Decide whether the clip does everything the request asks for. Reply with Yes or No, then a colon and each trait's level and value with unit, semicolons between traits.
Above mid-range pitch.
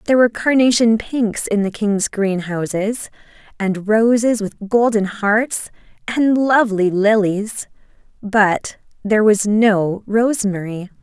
Yes: high, 215 Hz